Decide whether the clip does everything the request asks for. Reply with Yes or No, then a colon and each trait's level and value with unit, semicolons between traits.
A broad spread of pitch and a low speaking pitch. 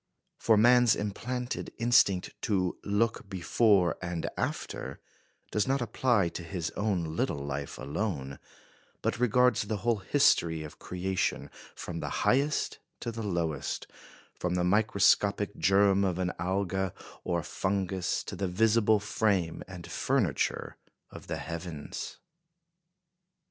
No: average, 3.9 semitones; very low, 95 Hz